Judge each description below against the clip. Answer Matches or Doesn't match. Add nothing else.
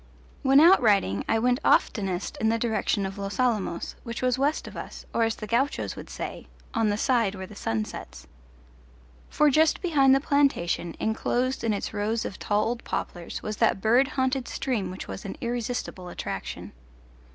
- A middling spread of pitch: Matches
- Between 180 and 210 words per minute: Matches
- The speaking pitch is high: Matches